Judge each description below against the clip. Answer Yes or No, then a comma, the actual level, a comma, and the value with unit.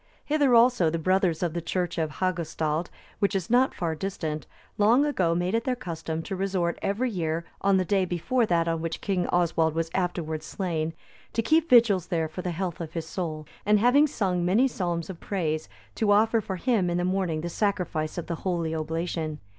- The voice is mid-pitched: Yes, medium, 180 Hz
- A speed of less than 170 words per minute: No, average, 200 wpm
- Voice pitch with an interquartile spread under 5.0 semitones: Yes, average, 3.6 semitones